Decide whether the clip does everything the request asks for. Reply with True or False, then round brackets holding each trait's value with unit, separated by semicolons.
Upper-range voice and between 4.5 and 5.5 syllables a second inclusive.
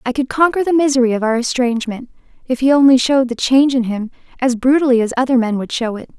False (255 Hz; 6.7 syllables/s)